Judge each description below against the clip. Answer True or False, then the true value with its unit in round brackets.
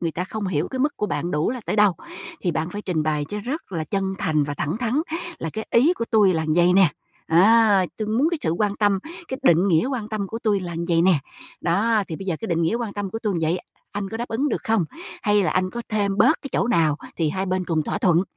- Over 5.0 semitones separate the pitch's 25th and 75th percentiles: False (4.6 semitones)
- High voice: True (195 Hz)